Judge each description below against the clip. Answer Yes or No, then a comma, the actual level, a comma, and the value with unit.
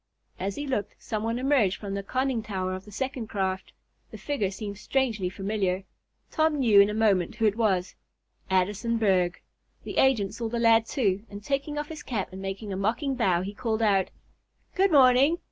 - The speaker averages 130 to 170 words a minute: No, average, 195 wpm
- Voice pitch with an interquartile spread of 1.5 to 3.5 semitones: No, average, 4.7 semitones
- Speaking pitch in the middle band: No, high, 215 Hz